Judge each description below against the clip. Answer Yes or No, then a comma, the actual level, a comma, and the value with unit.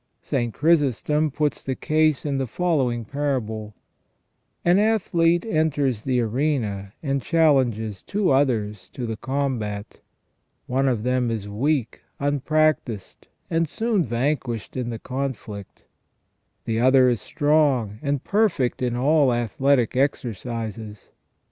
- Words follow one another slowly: Yes, slow, 130 wpm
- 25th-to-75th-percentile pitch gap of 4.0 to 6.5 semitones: Yes, average, 4.7 semitones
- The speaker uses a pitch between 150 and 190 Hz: No, low, 130 Hz